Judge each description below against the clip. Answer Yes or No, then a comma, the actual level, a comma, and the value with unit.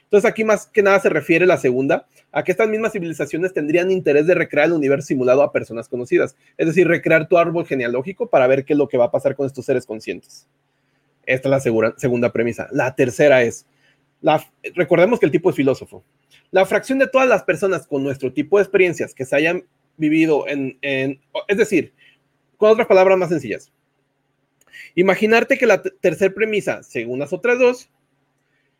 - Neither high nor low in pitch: Yes, medium, 155 Hz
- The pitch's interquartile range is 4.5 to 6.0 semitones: Yes, wide, 5.5 semitones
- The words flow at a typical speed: No, fast, 195 wpm